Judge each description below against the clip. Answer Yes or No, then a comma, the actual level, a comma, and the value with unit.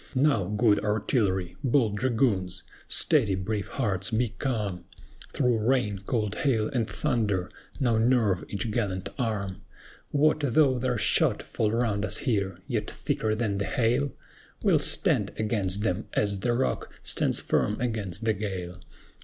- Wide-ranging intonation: No, average, 3.7 semitones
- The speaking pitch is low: Yes, low, 110 Hz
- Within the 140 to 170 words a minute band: Yes, average, 145 wpm